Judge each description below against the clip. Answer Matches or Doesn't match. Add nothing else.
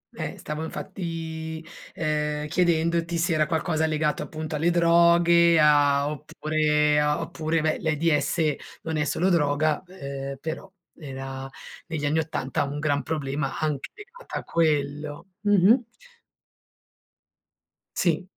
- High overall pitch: Doesn't match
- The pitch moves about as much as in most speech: Doesn't match